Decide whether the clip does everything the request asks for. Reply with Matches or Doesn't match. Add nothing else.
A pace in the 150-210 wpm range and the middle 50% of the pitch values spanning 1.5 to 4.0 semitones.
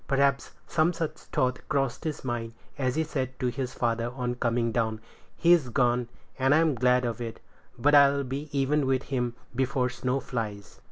Matches